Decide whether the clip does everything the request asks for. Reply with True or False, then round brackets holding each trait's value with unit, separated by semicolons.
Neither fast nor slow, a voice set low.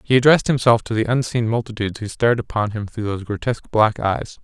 False (215 wpm; 115 Hz)